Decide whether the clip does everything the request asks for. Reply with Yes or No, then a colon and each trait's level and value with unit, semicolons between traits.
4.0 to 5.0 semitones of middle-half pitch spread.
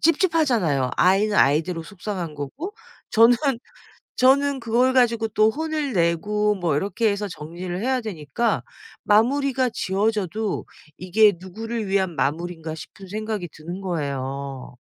No: wide, 5.5 semitones